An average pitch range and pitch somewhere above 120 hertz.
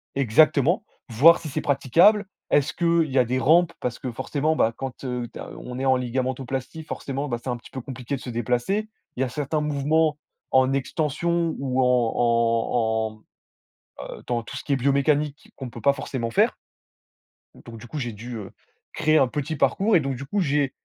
Yes: average, 3.7 semitones; low, 135 Hz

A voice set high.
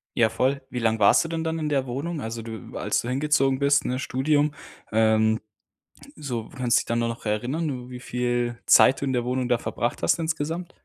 No: low, 125 Hz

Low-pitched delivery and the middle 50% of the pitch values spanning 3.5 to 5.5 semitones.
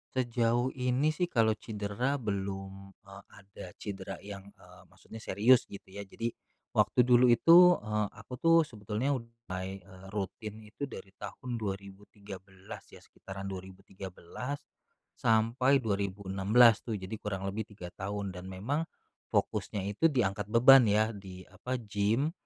Yes: low, 105 Hz; average, 3.9 semitones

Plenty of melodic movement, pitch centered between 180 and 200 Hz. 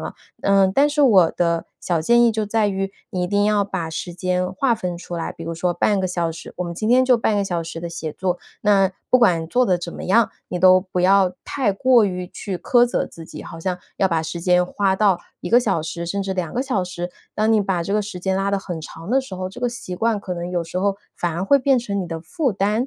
No: average, 3.4 semitones; high, 190 Hz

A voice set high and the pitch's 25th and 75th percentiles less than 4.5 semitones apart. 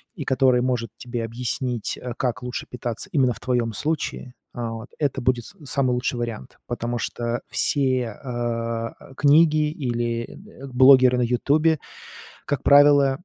No: low, 125 Hz; average, 2.7 semitones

